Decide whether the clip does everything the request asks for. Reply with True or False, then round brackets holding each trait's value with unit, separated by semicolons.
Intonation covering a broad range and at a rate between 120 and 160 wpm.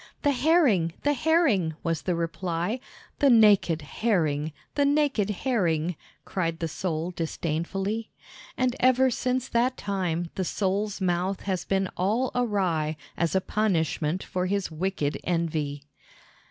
True (5.8 semitones; 140 wpm)